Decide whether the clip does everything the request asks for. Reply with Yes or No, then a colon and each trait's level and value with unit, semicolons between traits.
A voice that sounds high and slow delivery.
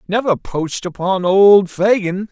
Yes: high, 195 Hz; slow, 130 wpm